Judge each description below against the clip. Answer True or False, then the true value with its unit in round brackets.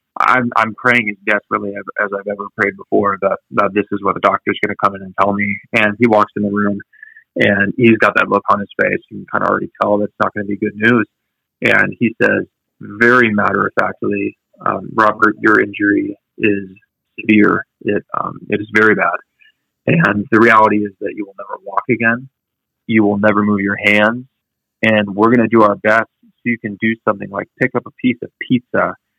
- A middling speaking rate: False (220 wpm)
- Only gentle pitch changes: True (2.1 semitones)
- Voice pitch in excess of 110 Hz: False (105 Hz)